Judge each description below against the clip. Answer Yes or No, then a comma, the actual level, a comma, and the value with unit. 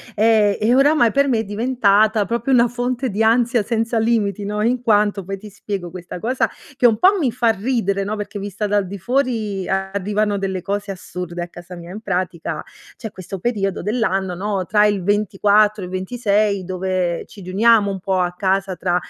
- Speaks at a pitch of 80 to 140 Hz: No, high, 205 Hz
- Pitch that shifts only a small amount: No, average, 3.0 semitones